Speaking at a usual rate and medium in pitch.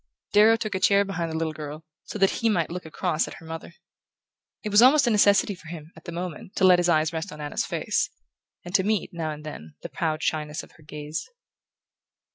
No: fast, 230 wpm; medium, 170 Hz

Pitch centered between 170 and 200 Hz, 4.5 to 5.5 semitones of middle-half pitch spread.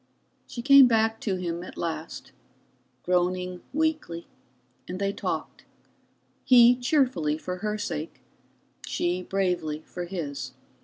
Yes: medium, 185 Hz; average, 5.1 semitones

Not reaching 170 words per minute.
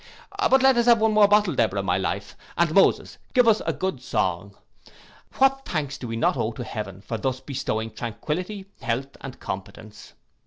No: average, 185 wpm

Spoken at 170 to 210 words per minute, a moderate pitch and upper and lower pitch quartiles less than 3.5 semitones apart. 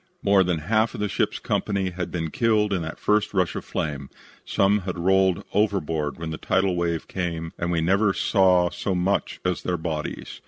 No: average, 190 wpm; very low, 90 Hz; average, 3.0 semitones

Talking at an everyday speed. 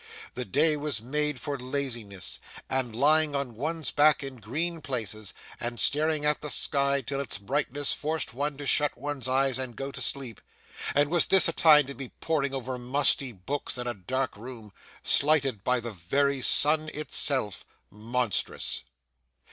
Yes: average, 165 wpm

